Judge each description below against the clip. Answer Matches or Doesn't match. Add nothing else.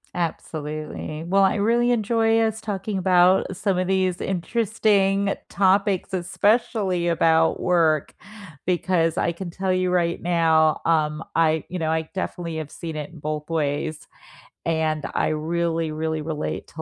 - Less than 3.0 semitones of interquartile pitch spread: Doesn't match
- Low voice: Doesn't match